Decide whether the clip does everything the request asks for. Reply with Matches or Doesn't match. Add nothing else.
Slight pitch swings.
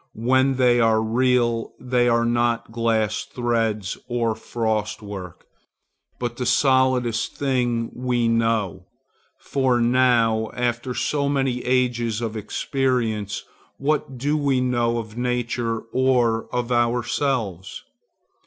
Matches